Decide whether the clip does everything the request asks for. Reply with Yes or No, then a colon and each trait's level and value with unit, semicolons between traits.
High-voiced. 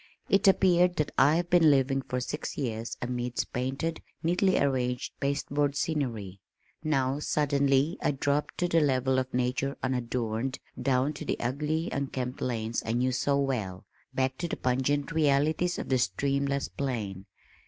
No: low, 135 Hz